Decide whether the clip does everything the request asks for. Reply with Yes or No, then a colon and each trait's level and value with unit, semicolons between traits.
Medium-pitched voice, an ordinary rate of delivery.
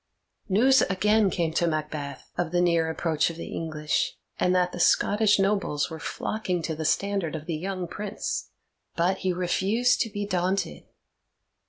Yes: medium, 180 Hz; average, 165 wpm